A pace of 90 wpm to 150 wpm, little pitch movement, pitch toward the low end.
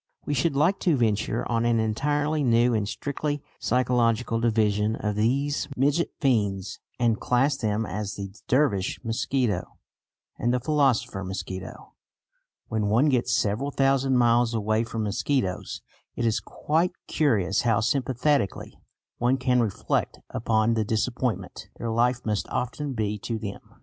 No: average, 140 wpm; average, 4.0 semitones; low, 120 Hz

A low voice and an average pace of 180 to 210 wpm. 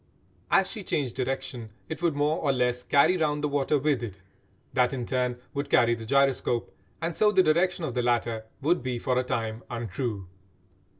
Yes: low, 130 Hz; average, 190 wpm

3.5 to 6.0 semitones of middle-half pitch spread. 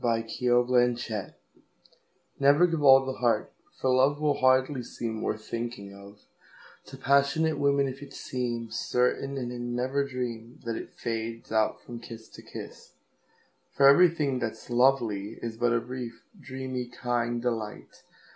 No: average, 2.7 semitones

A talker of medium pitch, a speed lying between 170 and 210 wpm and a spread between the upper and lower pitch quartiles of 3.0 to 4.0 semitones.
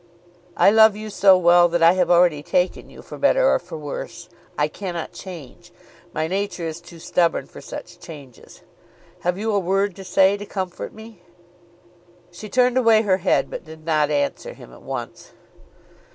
Yes: medium, 180 Hz; average, 180 wpm; average, 3.5 semitones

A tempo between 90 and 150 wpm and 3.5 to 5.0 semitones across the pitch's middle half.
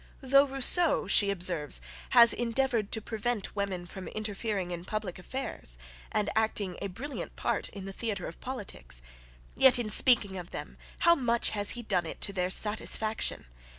No: average, 165 wpm; average, 4.3 semitones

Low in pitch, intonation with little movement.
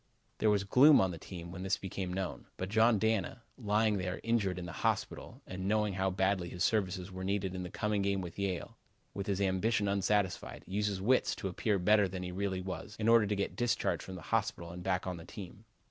Yes: very low, 95 Hz; narrow, 2.2 semitones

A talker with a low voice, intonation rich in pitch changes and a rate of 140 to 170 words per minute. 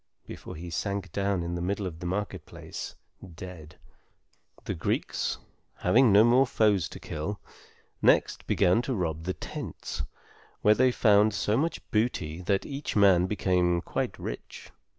No: very low, 95 Hz; average, 3.5 semitones; average, 150 wpm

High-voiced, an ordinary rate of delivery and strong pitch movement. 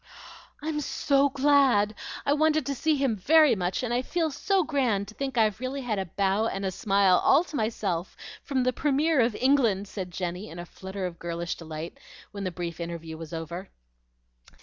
Yes: high, 215 Hz; average, 195 wpm; wide, 7.3 semitones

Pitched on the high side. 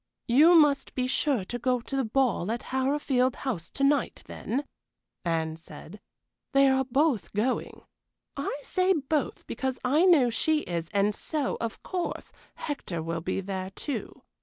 Yes: very high, 255 Hz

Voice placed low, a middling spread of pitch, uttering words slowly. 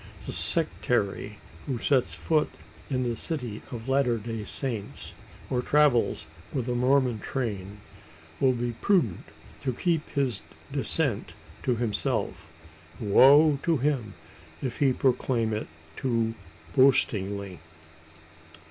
Yes: low, 125 Hz; average, 3.5 semitones; slow, 115 wpm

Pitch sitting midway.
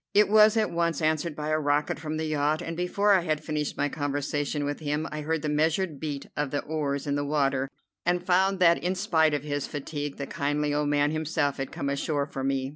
Yes: medium, 150 Hz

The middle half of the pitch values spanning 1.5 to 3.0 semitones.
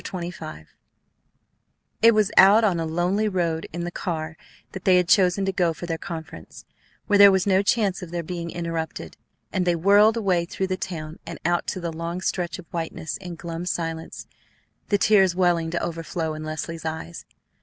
Yes: narrow, 2.5 semitones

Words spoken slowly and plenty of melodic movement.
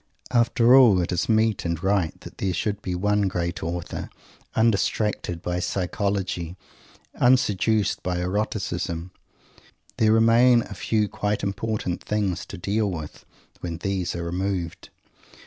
No: slow, 130 wpm; average, 3.5 semitones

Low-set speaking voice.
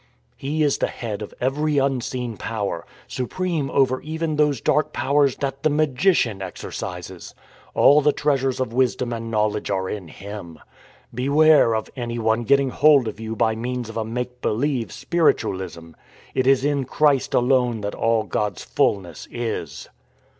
Yes: low, 125 Hz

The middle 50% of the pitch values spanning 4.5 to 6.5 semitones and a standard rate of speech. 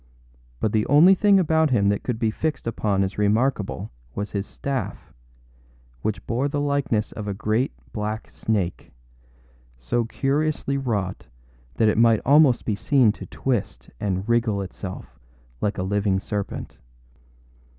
Yes: average, 5.0 semitones; average, 145 wpm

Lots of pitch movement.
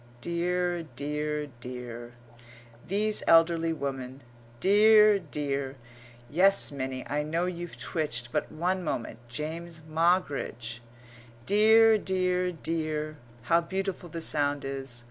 No: average, 4.5 semitones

